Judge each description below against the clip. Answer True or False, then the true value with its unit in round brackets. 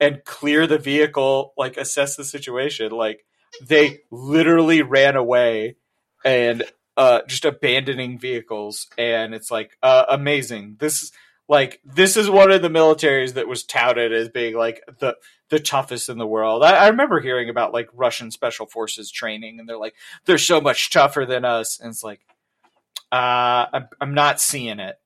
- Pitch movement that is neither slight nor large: True (4.2 semitones)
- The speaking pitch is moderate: False (125 Hz)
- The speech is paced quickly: False (170 wpm)